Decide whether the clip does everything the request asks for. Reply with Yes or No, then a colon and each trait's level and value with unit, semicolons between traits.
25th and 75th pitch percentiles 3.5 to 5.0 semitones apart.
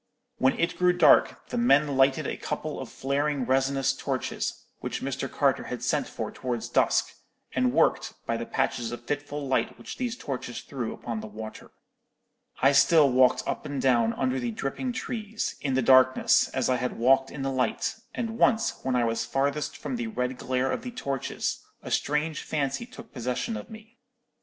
Yes: average, 3.8 semitones